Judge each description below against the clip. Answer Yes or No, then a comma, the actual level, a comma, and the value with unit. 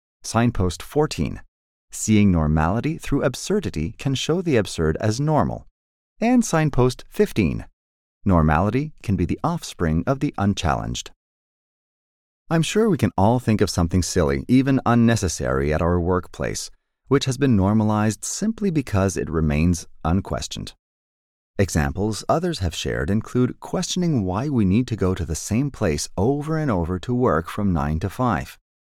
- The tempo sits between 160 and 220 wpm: No, average, 145 wpm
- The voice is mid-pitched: No, low, 105 Hz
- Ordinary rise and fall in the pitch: No, wide, 8.1 semitones